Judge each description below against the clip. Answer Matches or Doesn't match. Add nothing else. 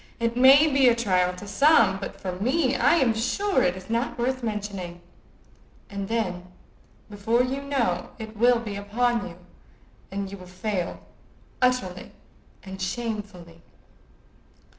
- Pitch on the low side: Doesn't match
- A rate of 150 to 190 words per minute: Doesn't match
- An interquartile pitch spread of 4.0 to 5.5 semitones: Matches